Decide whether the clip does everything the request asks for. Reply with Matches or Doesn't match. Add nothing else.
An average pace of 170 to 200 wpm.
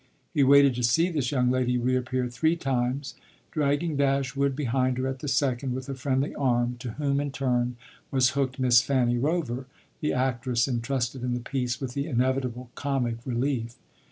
Matches